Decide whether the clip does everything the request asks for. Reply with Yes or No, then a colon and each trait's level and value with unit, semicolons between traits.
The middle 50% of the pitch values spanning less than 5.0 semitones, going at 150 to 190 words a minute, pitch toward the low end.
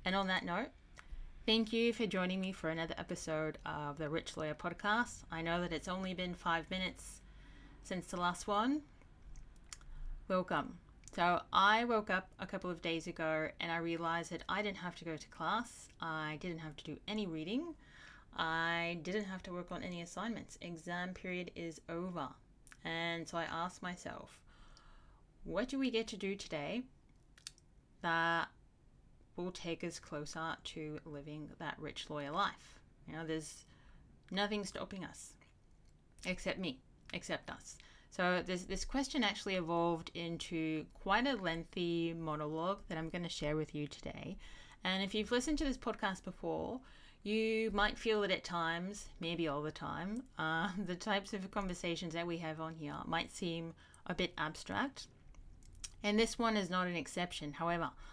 No: average, 3.4 semitones; average, 165 wpm; medium, 175 Hz